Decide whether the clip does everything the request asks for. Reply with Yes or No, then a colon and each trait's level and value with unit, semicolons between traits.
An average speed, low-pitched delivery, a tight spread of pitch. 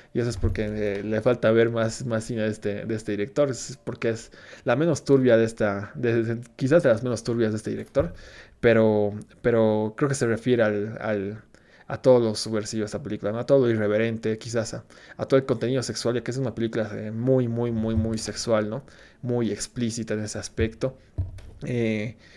No: fast, 210 wpm; low, 115 Hz; narrow, 2.1 semitones